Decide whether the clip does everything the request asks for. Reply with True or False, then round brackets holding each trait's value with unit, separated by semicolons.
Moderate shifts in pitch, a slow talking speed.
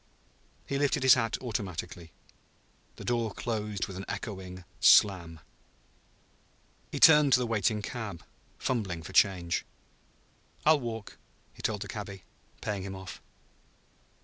True (4.0 semitones; 125 wpm)